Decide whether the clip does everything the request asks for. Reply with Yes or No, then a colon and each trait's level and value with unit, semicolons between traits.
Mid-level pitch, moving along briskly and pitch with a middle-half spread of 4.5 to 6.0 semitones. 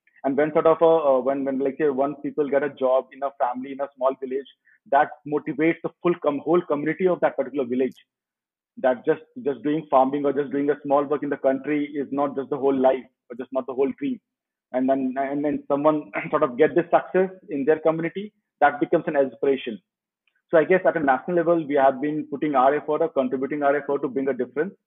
No: medium, 145 Hz; fast, 235 wpm; average, 2.8 semitones